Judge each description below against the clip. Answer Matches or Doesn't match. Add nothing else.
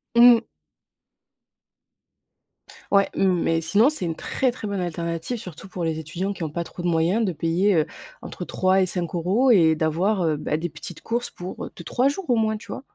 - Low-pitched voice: Doesn't match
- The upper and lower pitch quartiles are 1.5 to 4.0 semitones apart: Doesn't match